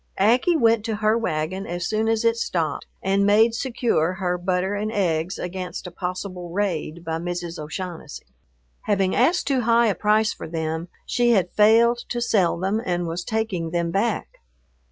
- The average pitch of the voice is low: No, high, 195 Hz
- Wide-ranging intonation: No, average, 4.2 semitones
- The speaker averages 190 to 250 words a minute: No, average, 175 wpm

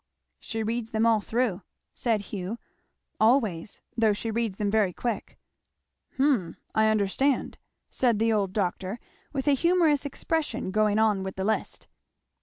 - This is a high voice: Yes, high, 220 Hz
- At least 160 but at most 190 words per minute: No, average, 145 wpm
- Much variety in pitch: No, average, 3.2 semitones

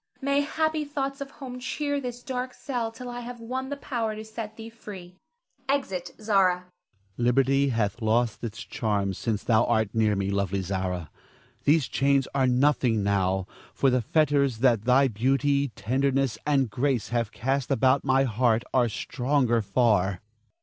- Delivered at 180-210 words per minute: No, average, 165 wpm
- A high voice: No, low, 135 Hz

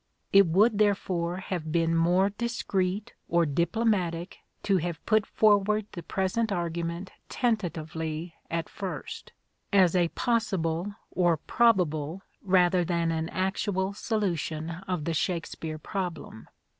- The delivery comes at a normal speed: No, slow, 120 wpm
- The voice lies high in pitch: No, medium, 180 Hz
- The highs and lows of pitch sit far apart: No, average, 3.2 semitones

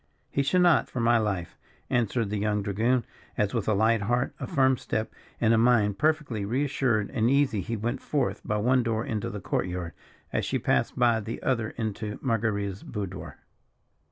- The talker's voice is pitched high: No, low, 115 Hz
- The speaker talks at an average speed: Yes, average, 190 wpm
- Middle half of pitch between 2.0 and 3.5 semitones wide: Yes, average, 3.0 semitones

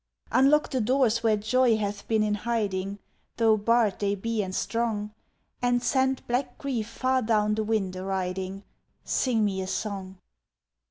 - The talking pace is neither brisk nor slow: Yes, average, 160 wpm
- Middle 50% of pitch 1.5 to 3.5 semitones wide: Yes, average, 3.1 semitones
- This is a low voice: No, high, 215 Hz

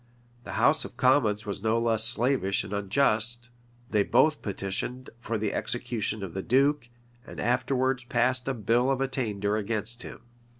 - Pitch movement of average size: Yes, average, 3.4 semitones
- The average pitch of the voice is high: No, low, 115 Hz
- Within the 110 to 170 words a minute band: Yes, average, 160 wpm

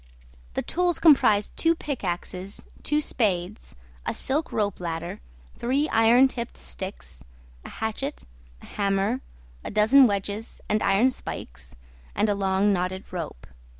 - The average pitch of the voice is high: Yes, high, 210 Hz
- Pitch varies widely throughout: Yes, wide, 5.7 semitones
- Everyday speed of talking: No, slow, 125 wpm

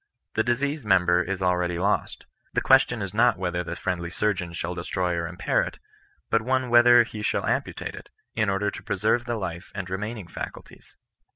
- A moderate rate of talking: Yes, average, 195 wpm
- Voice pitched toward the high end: No, very low, 95 Hz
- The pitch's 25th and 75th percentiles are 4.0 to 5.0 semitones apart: Yes, average, 4.6 semitones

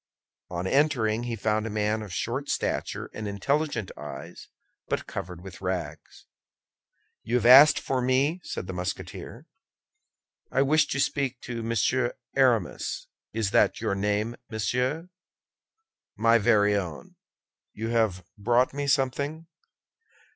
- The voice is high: No, low, 115 Hz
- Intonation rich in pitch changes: No, average, 4.6 semitones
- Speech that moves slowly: Yes, slow, 130 wpm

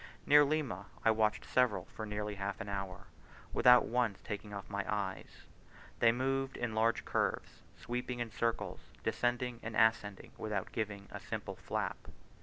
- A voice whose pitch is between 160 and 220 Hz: No, low, 110 Hz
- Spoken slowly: No, average, 155 wpm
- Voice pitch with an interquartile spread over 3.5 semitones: No, average, 3.2 semitones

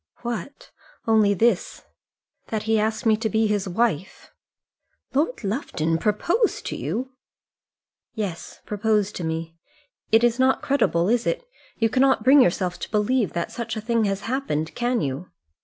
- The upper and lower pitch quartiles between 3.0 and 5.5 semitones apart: Yes, average, 3.8 semitones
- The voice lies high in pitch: Yes, high, 220 Hz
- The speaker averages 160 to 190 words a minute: No, average, 150 wpm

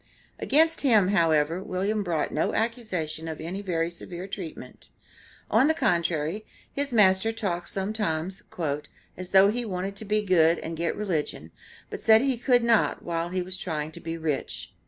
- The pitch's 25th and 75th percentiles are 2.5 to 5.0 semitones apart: Yes, average, 4.5 semitones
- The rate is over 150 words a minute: Yes, average, 165 wpm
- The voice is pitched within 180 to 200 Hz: Yes, medium, 185 Hz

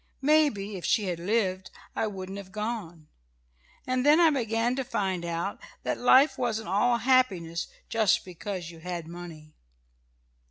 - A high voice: Yes, high, 200 Hz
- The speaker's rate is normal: Yes, average, 150 wpm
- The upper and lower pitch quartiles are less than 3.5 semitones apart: No, wide, 5.4 semitones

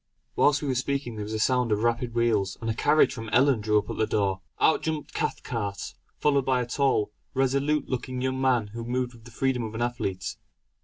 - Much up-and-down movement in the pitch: No, average, 3.2 semitones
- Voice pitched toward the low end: Yes, low, 120 Hz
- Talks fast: Yes, fast, 220 wpm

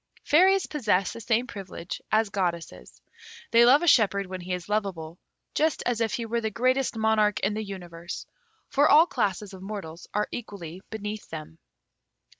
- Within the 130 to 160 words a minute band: No, average, 170 wpm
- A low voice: No, high, 210 Hz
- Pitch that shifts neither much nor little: Yes, average, 4.3 semitones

